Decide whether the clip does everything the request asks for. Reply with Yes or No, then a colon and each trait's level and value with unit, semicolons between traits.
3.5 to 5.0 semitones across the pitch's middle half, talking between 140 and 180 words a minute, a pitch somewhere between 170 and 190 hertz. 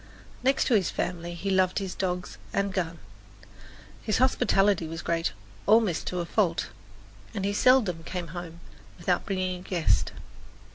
No: narrow, 2.6 semitones; average, 150 wpm; medium, 185 Hz